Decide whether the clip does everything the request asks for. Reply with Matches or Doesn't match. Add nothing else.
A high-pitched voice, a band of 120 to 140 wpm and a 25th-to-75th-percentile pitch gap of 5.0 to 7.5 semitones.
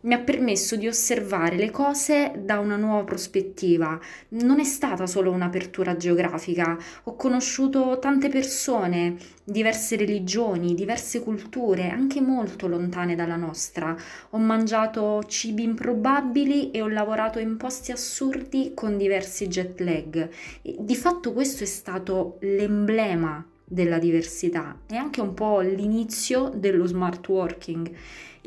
Matches